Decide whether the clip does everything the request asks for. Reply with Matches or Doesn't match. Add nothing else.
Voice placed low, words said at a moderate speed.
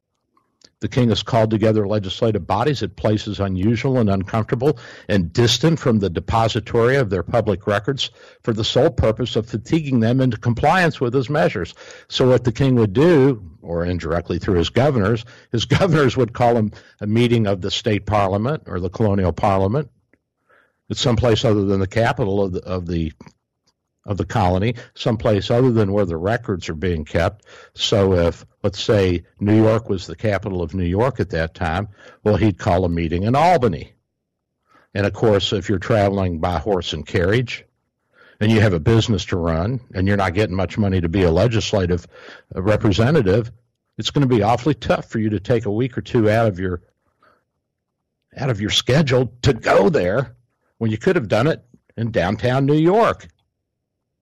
Matches